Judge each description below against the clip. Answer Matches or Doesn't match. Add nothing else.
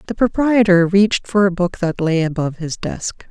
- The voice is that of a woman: Matches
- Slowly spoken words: Doesn't match